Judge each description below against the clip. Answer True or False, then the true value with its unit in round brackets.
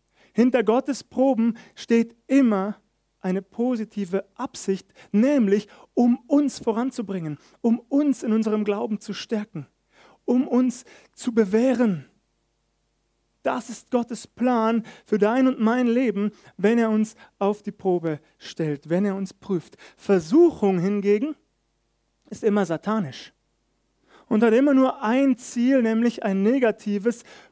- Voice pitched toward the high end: True (220 Hz)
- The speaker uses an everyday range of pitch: True (3.7 semitones)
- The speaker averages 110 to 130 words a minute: True (125 wpm)